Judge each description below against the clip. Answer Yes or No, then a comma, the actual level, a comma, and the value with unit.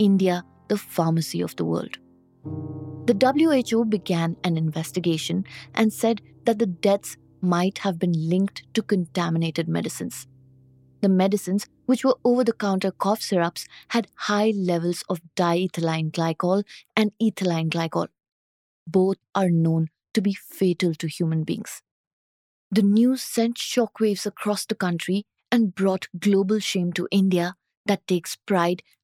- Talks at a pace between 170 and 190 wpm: No, slow, 135 wpm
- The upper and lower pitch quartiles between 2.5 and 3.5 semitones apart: No, average, 4.0 semitones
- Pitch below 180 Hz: No, medium, 185 Hz